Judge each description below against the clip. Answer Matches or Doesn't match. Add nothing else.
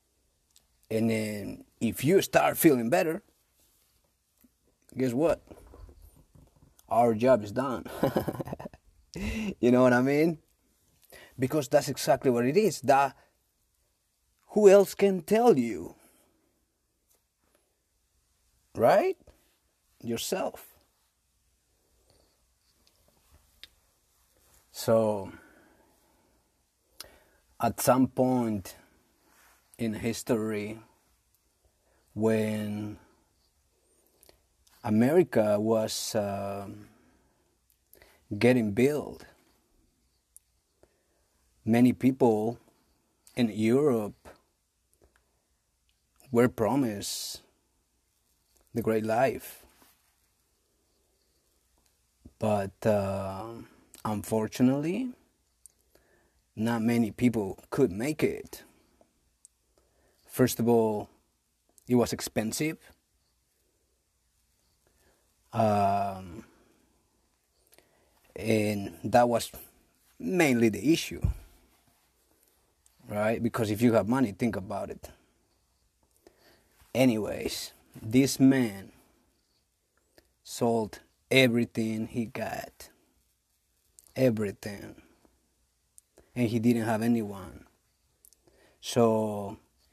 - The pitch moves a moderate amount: Doesn't match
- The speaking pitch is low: Matches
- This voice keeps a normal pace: Doesn't match